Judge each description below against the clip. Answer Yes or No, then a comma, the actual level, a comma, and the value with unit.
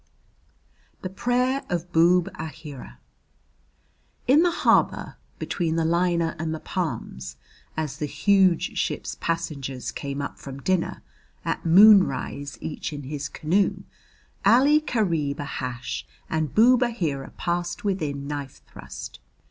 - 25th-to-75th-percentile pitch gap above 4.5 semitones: Yes, average, 5.1 semitones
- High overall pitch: No, medium, 165 Hz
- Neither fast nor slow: No, slow, 120 wpm